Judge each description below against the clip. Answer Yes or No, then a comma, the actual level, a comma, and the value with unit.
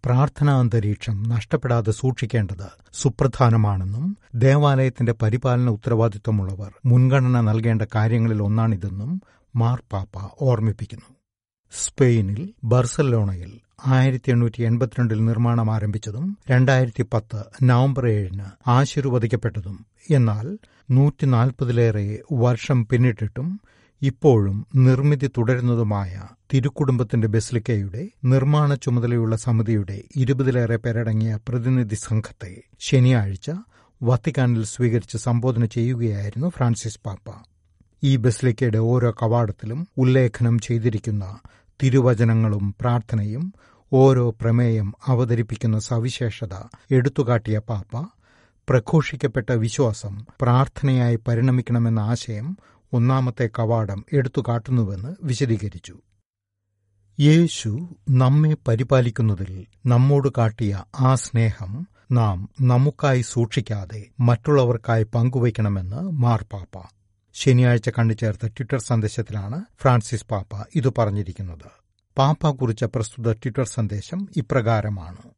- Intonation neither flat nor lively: Yes, average, 3.1 semitones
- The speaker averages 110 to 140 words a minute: No, average, 80 wpm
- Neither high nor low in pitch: No, low, 120 Hz